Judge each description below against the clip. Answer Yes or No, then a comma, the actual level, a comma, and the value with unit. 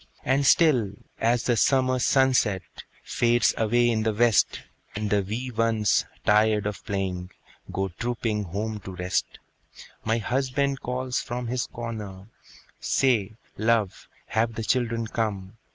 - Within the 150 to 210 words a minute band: No, slow, 135 wpm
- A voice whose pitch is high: No, low, 115 Hz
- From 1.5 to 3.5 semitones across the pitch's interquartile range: Yes, average, 2.8 semitones